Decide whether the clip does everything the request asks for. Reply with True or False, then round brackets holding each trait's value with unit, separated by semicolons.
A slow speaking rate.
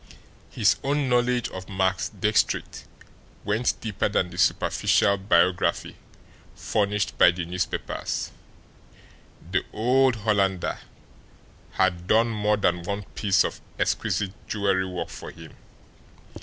True (115 wpm)